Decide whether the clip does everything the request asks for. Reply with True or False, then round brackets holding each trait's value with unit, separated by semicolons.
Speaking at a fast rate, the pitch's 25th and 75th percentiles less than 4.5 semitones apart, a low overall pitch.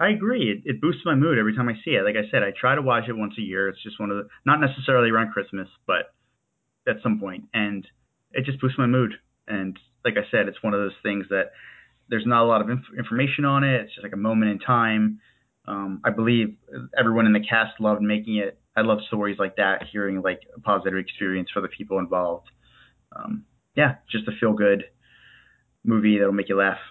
True (230 wpm; 3.7 semitones; 110 Hz)